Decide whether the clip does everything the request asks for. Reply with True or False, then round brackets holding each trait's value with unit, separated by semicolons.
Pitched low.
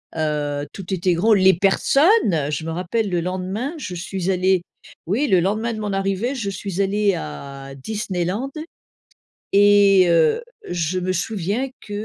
False (190 Hz)